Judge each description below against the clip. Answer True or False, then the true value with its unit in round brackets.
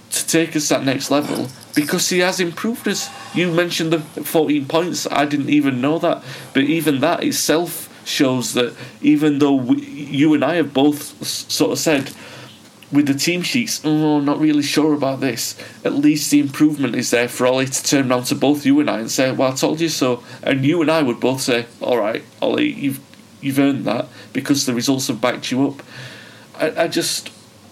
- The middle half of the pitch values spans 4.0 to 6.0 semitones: False (3.5 semitones)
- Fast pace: True (210 wpm)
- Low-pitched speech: False (145 Hz)